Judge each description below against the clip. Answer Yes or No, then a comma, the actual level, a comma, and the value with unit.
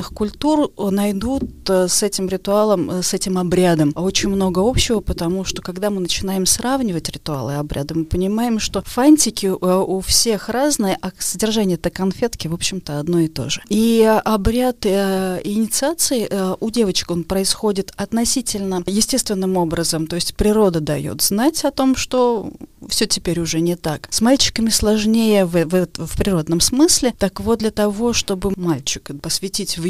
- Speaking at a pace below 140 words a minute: No, average, 155 wpm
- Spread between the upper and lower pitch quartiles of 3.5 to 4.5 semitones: Yes, average, 3.8 semitones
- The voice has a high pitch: Yes, high, 195 Hz